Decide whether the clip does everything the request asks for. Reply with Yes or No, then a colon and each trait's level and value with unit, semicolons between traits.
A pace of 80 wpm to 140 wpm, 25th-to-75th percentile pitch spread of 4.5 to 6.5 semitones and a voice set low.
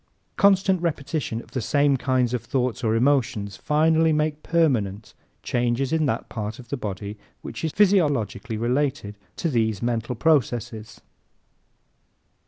Yes: slow, 135 wpm; average, 5.2 semitones; low, 125 Hz